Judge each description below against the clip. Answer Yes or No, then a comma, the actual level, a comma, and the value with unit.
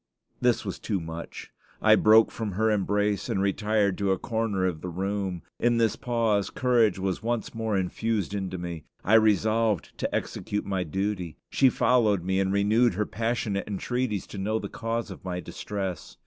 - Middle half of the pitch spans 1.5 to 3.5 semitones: Yes, average, 2.9 semitones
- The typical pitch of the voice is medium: No, low, 105 Hz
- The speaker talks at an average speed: Yes, average, 175 wpm